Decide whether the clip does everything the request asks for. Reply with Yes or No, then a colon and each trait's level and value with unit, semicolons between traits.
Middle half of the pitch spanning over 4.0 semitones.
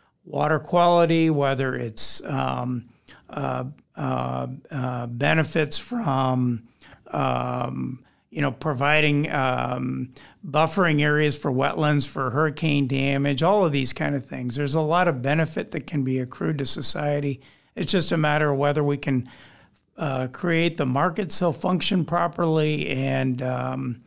No: average, 3.5 semitones